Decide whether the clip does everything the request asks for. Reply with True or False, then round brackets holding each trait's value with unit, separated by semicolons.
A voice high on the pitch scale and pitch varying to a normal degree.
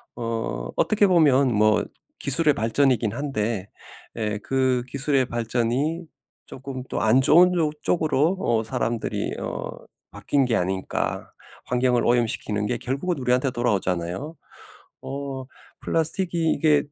False (130 Hz; 4.5 semitones)